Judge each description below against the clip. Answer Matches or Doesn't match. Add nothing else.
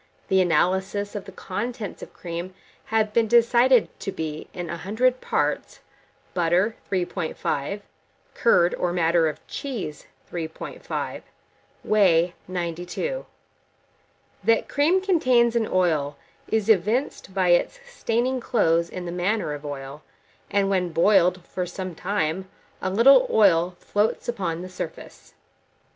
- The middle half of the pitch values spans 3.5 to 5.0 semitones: Matches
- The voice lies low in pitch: Doesn't match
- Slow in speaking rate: Matches